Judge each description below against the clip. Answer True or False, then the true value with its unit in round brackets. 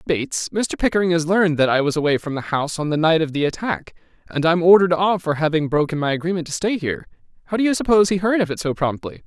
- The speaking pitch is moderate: True (165 Hz)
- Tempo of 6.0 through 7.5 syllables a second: True (7.0 syllables/s)